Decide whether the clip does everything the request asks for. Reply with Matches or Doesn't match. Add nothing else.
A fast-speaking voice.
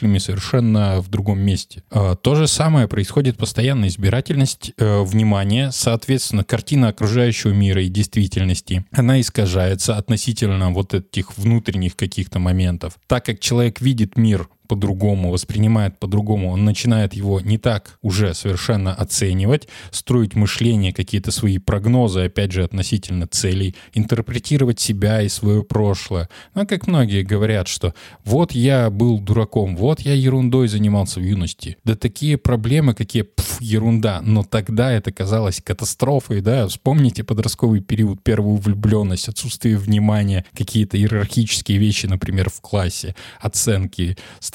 Doesn't match